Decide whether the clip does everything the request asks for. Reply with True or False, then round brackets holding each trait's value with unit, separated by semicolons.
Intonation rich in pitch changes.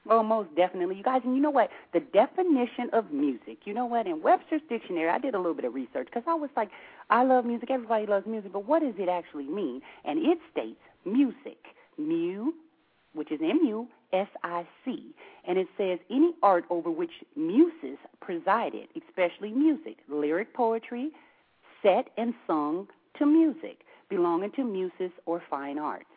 True (8.4 semitones)